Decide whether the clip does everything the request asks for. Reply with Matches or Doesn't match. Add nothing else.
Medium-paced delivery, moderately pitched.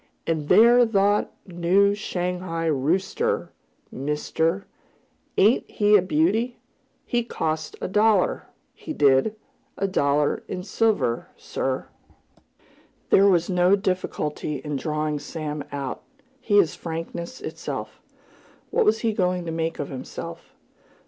Doesn't match